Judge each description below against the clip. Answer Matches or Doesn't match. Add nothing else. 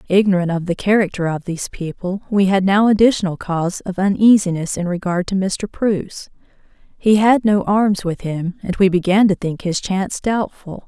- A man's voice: Doesn't match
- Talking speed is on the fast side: Doesn't match